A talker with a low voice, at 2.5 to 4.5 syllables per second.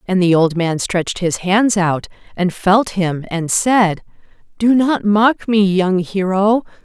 No: high, 195 Hz; 3.7 syllables/s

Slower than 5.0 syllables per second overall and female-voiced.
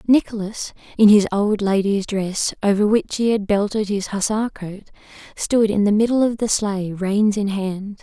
Yes: 4.7 syllables/s; female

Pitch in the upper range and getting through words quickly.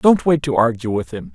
No: low, 125 Hz; fast, 270 wpm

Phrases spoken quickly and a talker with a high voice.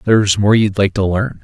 No: fast, 250 wpm; low, 100 Hz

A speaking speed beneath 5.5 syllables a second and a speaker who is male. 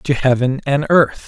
Yes: 4.4 syllables/s; male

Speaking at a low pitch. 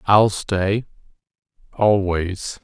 Yes: low, 100 Hz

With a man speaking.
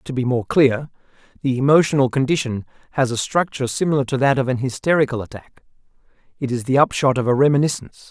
Yes: male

